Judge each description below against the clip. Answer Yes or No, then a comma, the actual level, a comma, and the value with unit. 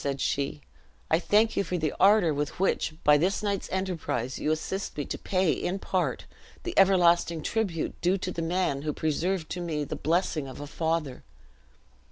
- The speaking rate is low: No, average, 185 wpm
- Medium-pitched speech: Yes, medium, 170 Hz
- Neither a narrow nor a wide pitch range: Yes, average, 4.0 semitones